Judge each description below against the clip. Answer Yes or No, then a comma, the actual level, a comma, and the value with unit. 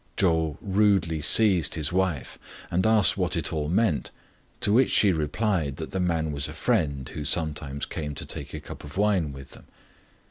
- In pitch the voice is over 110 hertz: No, very low, 80 Hz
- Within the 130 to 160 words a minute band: No, average, 185 wpm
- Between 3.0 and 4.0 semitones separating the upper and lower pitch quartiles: No, average, 4.4 semitones